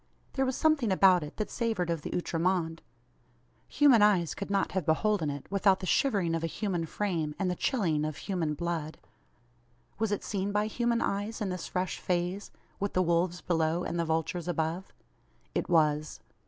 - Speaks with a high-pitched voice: No, medium, 180 Hz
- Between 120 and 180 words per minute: No, average, 190 wpm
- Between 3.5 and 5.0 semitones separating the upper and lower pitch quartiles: Yes, average, 3.8 semitones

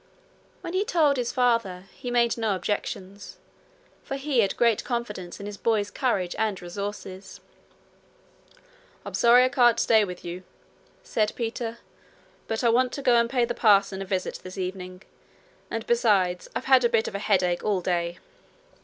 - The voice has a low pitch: No, high, 220 Hz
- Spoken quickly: No, average, 170 wpm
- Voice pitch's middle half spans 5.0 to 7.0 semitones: No, average, 4.1 semitones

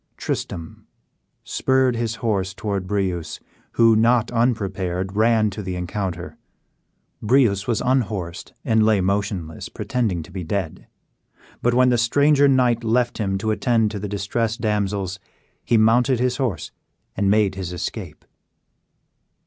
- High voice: No, low, 105 Hz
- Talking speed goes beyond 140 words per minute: No, slow, 135 wpm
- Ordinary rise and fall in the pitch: Yes, average, 3.6 semitones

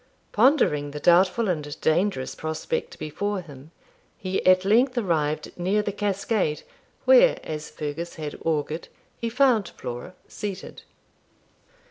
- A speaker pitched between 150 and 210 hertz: Yes, medium, 185 Hz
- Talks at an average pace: No, slow, 120 wpm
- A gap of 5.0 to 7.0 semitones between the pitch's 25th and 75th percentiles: Yes, wide, 5.4 semitones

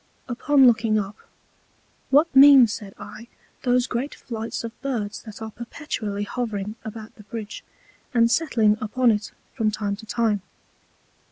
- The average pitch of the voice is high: Yes, high, 225 Hz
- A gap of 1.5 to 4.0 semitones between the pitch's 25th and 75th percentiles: Yes, average, 2.8 semitones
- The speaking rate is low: No, average, 145 wpm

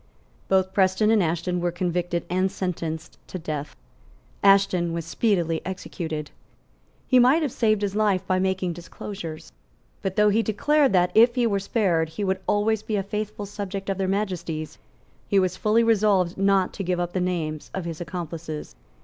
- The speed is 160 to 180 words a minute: Yes, average, 175 wpm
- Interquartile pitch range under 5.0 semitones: Yes, average, 3.1 semitones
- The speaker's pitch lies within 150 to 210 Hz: Yes, high, 190 Hz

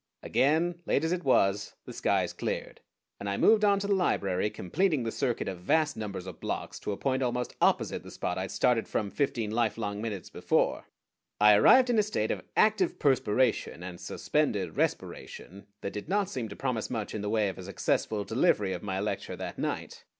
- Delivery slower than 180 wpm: No, average, 200 wpm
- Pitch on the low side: Yes, low, 110 Hz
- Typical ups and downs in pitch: No, wide, 6.7 semitones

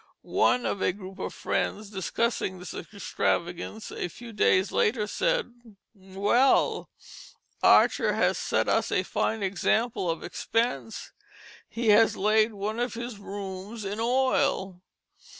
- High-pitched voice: Yes, high, 210 Hz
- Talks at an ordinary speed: No, slow, 130 wpm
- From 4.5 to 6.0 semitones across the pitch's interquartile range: No, average, 3.3 semitones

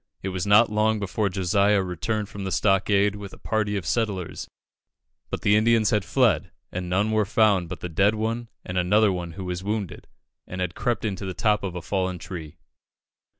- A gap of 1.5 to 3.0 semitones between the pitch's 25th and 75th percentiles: Yes, average, 2.7 semitones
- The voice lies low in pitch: Yes, low, 100 Hz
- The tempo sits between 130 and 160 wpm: No, average, 195 wpm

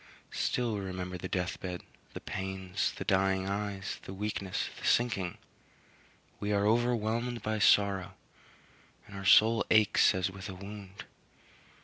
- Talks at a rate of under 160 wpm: Yes, average, 140 wpm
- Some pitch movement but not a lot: No, narrow, 2.1 semitones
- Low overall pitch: Yes, low, 100 Hz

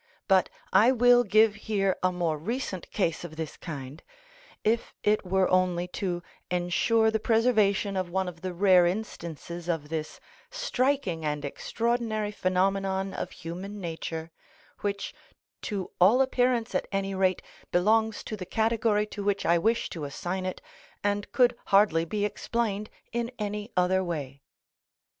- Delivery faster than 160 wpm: No, average, 150 wpm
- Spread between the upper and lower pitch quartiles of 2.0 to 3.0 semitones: No, average, 3.7 semitones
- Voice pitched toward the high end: Yes, high, 195 Hz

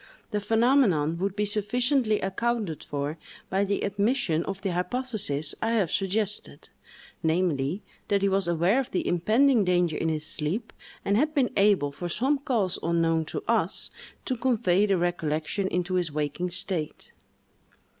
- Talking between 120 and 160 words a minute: Yes, average, 155 wpm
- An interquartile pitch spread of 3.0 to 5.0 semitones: Yes, average, 4.7 semitones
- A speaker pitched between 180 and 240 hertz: Yes, high, 190 Hz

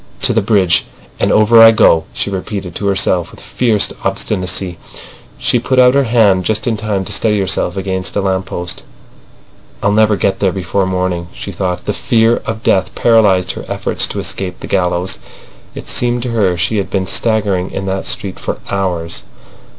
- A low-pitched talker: Yes, low, 100 Hz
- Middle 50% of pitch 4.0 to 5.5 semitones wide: No, average, 2.9 semitones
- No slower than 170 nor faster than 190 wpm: Yes, average, 180 wpm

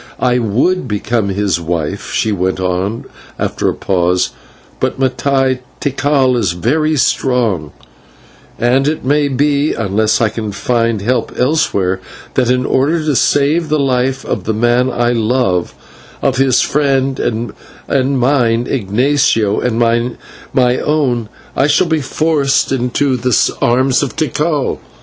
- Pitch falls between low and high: No, low, 125 Hz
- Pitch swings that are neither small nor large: Yes, average, 3.8 semitones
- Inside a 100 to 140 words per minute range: Yes, slow, 135 wpm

